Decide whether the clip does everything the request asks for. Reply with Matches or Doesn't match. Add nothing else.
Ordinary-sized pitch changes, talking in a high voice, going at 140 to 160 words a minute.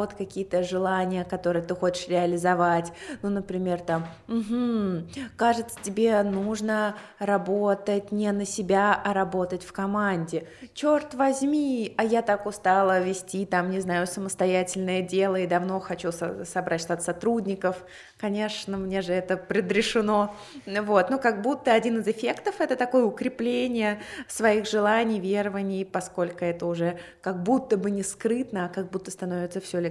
Matches